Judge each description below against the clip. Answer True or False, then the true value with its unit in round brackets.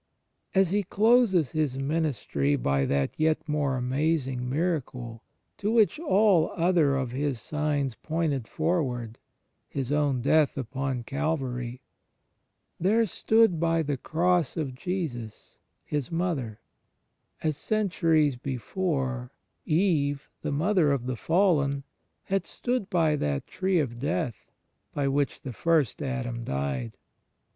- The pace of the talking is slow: True (130 wpm)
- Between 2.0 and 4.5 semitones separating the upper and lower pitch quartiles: False (4.9 semitones)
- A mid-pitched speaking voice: True (145 Hz)